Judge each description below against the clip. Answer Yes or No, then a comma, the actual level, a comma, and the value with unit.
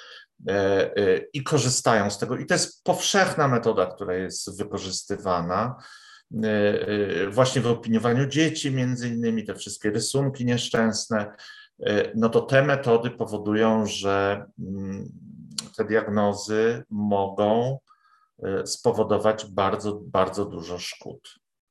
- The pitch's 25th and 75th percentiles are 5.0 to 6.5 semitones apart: Yes, wide, 5.4 semitones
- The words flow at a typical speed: No, slow, 100 wpm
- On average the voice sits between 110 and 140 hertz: Yes, low, 115 Hz